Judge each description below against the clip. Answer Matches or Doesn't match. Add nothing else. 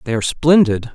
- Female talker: Doesn't match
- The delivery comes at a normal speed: Matches